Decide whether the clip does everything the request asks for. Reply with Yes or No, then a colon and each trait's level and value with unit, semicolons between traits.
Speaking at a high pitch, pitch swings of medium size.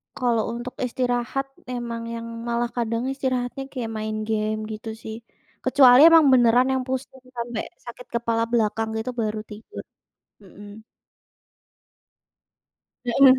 No: high, 240 Hz; narrow, 2.3 semitones